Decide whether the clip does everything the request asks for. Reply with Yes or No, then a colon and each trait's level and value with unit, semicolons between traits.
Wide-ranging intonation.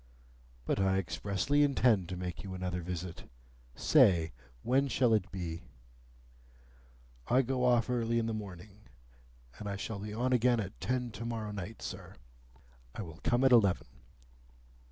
No: average, 4.8 semitones